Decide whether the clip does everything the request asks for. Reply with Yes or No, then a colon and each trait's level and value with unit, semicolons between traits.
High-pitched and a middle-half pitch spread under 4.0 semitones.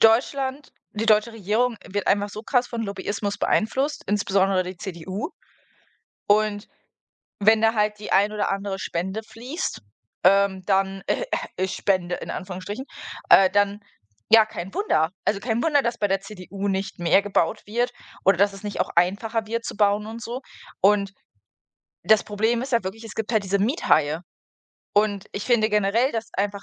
Yes: high, 205 Hz; narrow, 2.4 semitones